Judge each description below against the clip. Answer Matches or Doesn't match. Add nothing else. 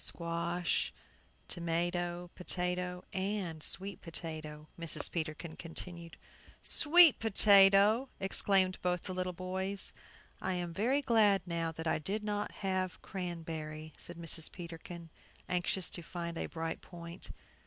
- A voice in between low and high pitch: Matches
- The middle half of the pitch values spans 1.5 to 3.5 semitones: Matches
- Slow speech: Matches